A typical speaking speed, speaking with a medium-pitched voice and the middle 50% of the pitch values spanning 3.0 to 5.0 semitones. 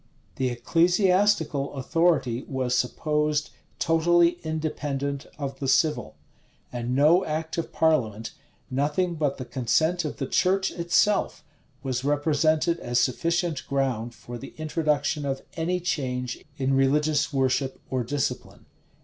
No: slow, 125 wpm; medium, 145 Hz; average, 3.7 semitones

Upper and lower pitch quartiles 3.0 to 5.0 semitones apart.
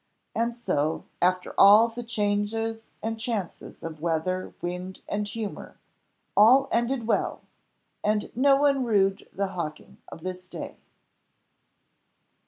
Yes: average, 4.0 semitones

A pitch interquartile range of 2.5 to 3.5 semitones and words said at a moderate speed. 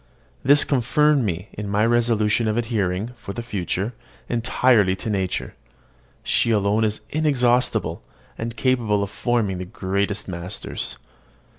No: average, 3.2 semitones; slow, 130 wpm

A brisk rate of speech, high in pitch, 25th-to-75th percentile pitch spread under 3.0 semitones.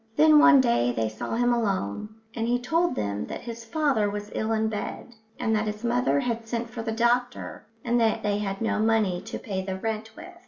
Yes: fast, 220 wpm; high, 225 Hz; narrow, 2.6 semitones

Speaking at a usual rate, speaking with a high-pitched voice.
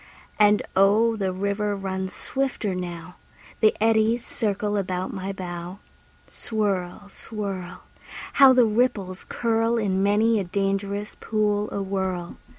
No: slow, 120 wpm; high, 200 Hz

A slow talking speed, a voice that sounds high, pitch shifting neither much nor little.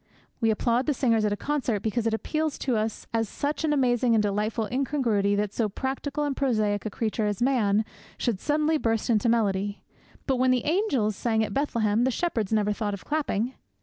No: average, 200 wpm; high, 230 Hz; average, 4.1 semitones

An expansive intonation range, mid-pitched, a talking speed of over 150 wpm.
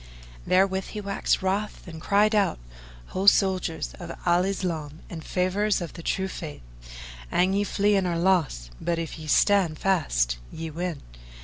No: average, 3.3 semitones; medium, 180 Hz; average, 165 wpm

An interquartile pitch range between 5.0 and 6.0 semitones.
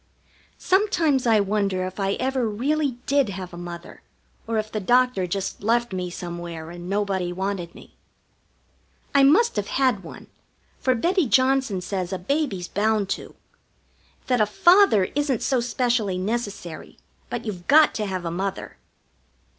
Yes: wide, 5.6 semitones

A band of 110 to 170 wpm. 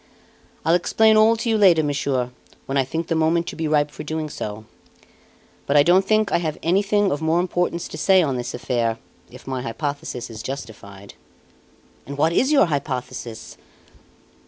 No: average, 180 wpm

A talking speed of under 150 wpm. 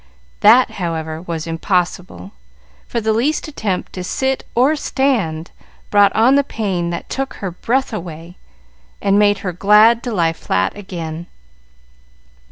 Yes: average, 140 wpm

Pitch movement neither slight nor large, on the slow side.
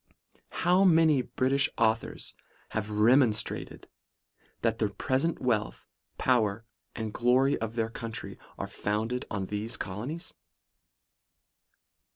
Yes: average, 3.6 semitones; slow, 110 wpm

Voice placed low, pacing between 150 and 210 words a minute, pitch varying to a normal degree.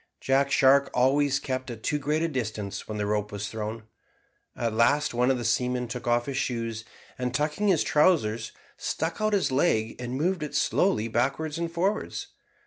Yes: low, 130 Hz; average, 190 wpm; average, 4.6 semitones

